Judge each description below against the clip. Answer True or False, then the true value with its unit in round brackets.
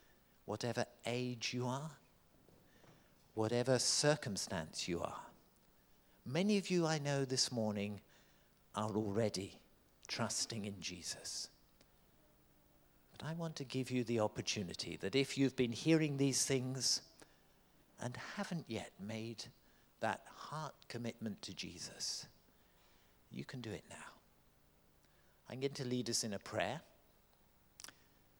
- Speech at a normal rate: False (120 wpm)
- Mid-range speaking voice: False (125 Hz)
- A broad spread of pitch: False (3.9 semitones)